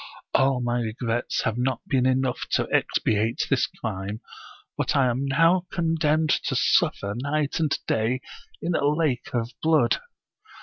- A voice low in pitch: Yes, low, 130 Hz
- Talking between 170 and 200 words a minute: No, average, 145 wpm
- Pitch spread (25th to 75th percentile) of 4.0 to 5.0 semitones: Yes, average, 4.3 semitones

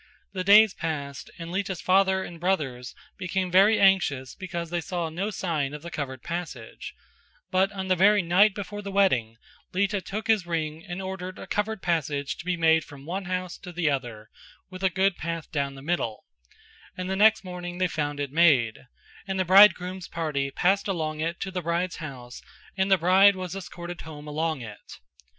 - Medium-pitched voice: Yes, medium, 175 Hz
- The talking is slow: No, average, 195 wpm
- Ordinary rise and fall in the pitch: Yes, average, 3.7 semitones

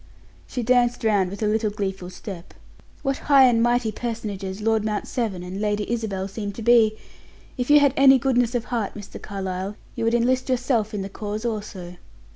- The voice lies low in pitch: No, high, 220 Hz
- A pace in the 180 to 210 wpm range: Yes, average, 190 wpm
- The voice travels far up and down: No, average, 3.2 semitones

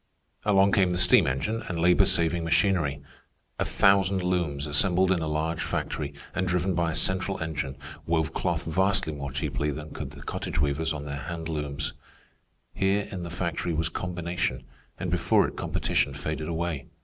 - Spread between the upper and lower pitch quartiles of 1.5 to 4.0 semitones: Yes, average, 3.4 semitones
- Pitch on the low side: Yes, very low, 85 Hz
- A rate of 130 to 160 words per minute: No, average, 175 wpm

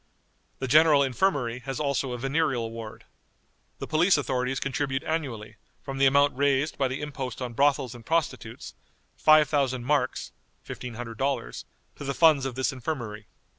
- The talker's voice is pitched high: No, low, 135 Hz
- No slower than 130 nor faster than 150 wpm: Yes, average, 145 wpm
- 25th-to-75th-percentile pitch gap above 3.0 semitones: No, average, 2.7 semitones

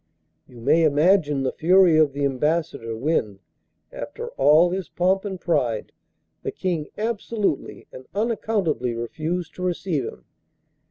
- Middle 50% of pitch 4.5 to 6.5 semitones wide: Yes, average, 5.3 semitones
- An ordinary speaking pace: No, slow, 130 wpm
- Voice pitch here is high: No, medium, 160 Hz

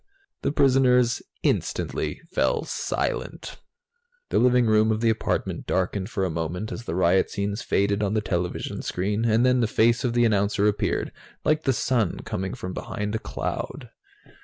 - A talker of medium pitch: No, low, 110 Hz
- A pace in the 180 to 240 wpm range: No, average, 165 wpm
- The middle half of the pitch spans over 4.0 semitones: No, average, 3.5 semitones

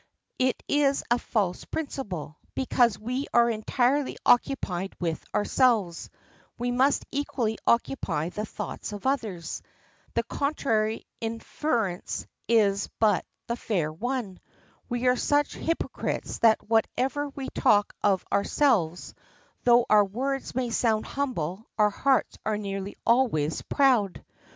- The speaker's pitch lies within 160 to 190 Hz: No, high, 230 Hz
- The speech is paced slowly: Yes, slow, 120 wpm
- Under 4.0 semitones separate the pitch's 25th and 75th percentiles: No, average, 4.6 semitones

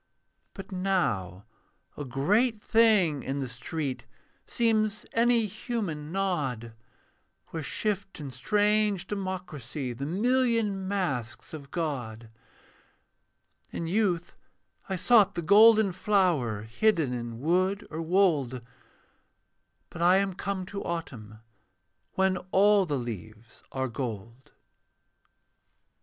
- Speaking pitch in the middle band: Yes, medium, 175 Hz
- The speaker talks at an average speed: No, slow, 105 wpm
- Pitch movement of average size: No, wide, 7.3 semitones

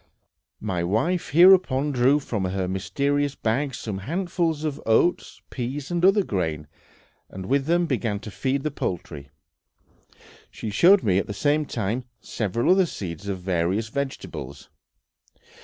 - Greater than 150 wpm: No, average, 140 wpm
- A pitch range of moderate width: No, wide, 7.6 semitones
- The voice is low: Yes, low, 125 Hz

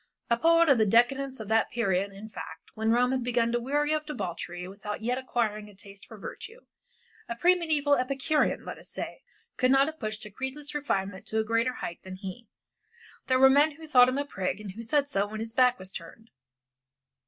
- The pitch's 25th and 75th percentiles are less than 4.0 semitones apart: No, average, 4.8 semitones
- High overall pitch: Yes, high, 235 Hz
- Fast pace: Yes, fast, 215 wpm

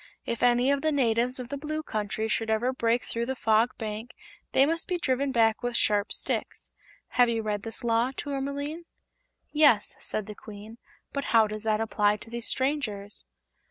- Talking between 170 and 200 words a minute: Yes, average, 185 wpm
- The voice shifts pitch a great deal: No, average, 3.8 semitones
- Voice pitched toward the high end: Yes, high, 235 Hz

